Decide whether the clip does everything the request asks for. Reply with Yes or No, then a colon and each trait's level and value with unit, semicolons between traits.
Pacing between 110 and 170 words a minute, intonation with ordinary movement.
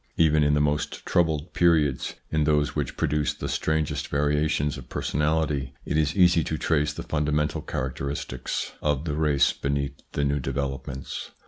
No: average, 155 wpm; narrow, 1.6 semitones